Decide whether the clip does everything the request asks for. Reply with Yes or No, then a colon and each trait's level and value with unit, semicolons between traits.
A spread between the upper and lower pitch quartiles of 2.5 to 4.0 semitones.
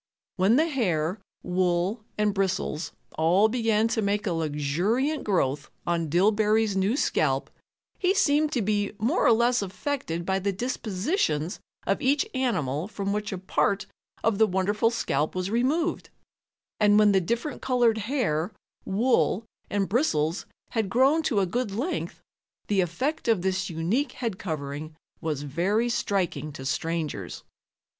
No: average, 5.3 semitones